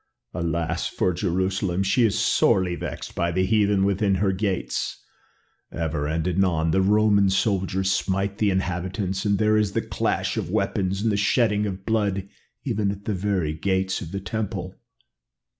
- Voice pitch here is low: Yes, very low, 95 Hz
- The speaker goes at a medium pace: Yes, average, 160 wpm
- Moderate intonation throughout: No, narrow, 2.0 semitones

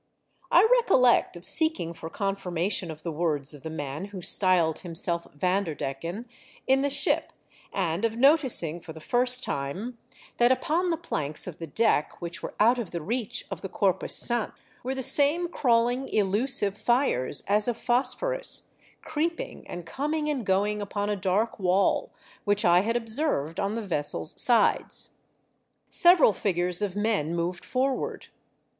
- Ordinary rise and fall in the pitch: No, wide, 6.6 semitones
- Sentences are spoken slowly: No, average, 155 wpm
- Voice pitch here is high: Yes, high, 205 Hz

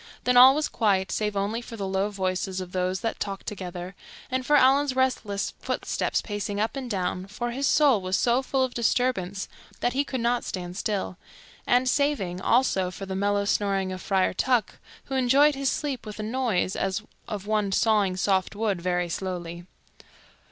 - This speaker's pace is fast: No, average, 185 wpm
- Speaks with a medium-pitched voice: No, high, 205 Hz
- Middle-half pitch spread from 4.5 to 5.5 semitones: Yes, average, 4.9 semitones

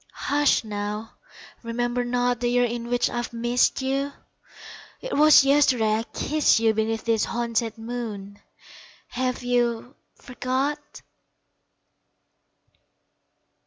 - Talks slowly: Yes, slow, 95 wpm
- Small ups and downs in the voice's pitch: Yes, narrow, 1.9 semitones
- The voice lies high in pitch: Yes, high, 245 Hz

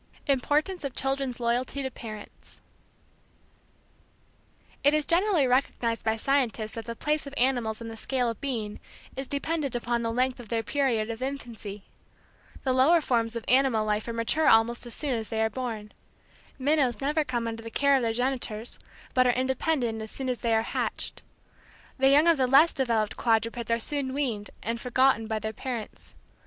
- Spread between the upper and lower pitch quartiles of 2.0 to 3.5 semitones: Yes, average, 3.2 semitones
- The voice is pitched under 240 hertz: No, high, 245 Hz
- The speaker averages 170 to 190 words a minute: Yes, average, 180 wpm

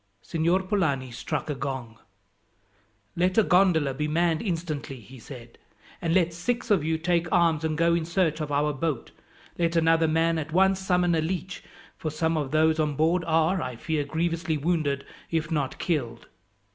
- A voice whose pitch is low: No, medium, 160 Hz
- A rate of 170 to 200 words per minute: Yes, average, 175 wpm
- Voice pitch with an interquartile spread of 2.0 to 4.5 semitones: Yes, narrow, 2.6 semitones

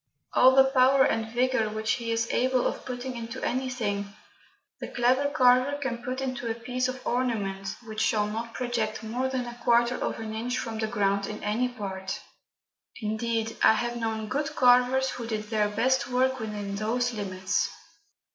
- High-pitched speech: Yes, high, 235 Hz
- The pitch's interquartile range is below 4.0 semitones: Yes, average, 2.7 semitones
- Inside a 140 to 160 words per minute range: No, average, 175 wpm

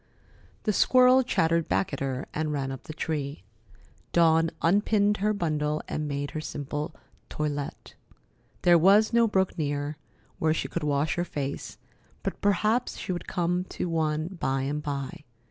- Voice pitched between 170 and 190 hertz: No, medium, 160 Hz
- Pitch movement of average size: Yes, average, 4.1 semitones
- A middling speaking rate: Yes, average, 160 wpm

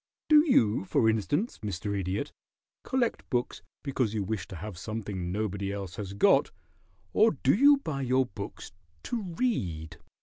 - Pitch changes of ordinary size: No, wide, 7.2 semitones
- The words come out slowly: No, average, 155 wpm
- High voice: No, low, 110 Hz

